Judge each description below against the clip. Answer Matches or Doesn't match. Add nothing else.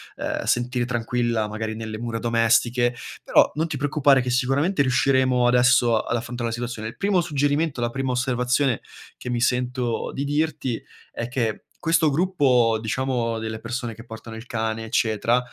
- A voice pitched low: Matches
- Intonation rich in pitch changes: Doesn't match